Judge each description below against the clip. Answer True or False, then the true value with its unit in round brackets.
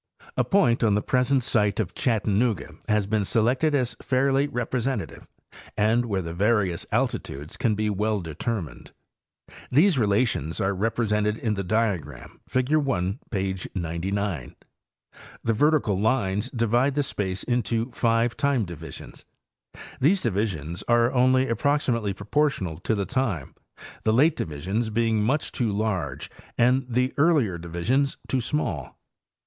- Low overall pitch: True (110 Hz)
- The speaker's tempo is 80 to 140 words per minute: True (135 wpm)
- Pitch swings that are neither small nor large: True (4.8 semitones)